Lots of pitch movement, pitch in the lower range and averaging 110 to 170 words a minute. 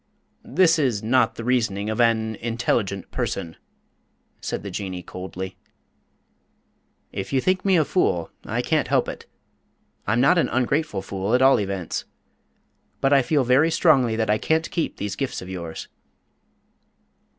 Yes: wide, 5.9 semitones; low, 115 Hz; average, 150 wpm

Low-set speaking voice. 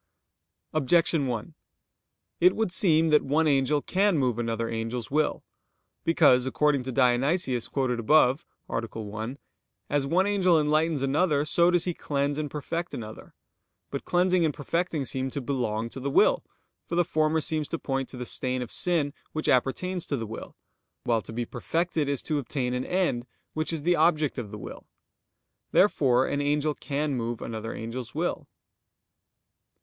No: medium, 145 Hz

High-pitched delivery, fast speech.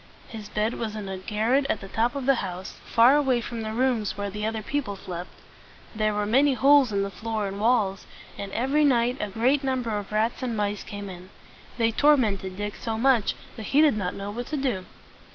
Yes: high, 220 Hz; fast, 225 wpm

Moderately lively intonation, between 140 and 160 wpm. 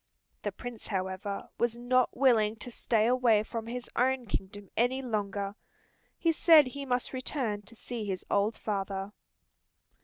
Yes: average, 3.6 semitones; average, 150 wpm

